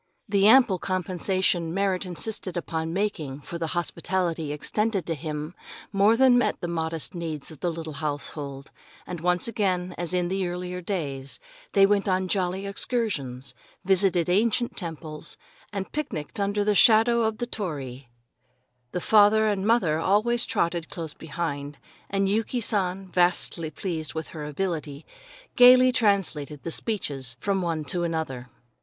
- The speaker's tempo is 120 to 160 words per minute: Yes, average, 150 wpm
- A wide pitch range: No, average, 4.1 semitones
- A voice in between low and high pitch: Yes, medium, 180 Hz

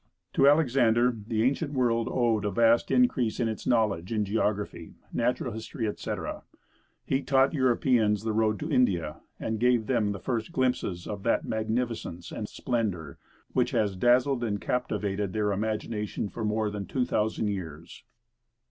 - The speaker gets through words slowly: No, average, 155 wpm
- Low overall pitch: Yes, low, 110 Hz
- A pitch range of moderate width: Yes, average, 3.1 semitones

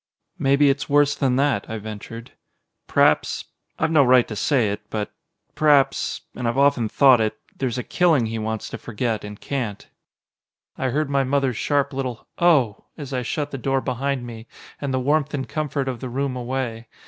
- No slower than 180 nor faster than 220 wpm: Yes, average, 185 wpm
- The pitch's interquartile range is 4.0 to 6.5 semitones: No, average, 3.3 semitones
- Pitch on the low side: Yes, low, 130 Hz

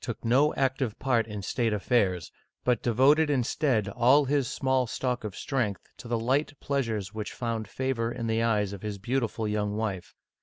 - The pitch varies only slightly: No, average, 3.7 semitones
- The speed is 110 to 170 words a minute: No, average, 185 wpm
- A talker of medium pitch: No, low, 115 Hz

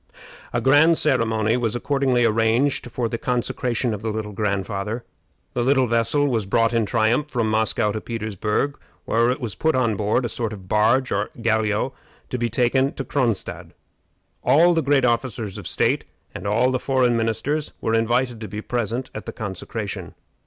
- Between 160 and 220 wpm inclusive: Yes, average, 175 wpm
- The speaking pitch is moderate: No, low, 115 Hz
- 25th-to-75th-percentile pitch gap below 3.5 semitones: Yes, average, 2.9 semitones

